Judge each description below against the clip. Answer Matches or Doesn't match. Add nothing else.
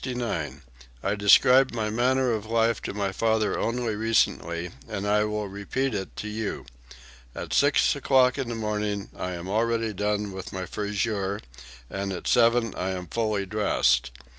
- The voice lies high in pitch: Doesn't match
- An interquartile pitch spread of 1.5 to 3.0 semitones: Matches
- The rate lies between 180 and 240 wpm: Doesn't match